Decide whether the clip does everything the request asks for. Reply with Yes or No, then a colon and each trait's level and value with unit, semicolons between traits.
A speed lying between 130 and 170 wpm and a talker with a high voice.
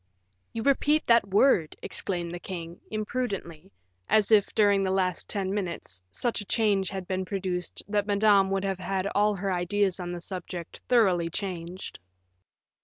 Yes: average, 160 wpm; high, 195 Hz